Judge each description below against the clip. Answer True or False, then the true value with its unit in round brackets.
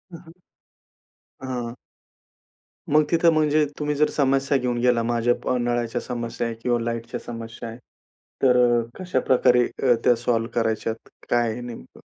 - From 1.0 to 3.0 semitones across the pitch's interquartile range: True (2.5 semitones)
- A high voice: False (120 Hz)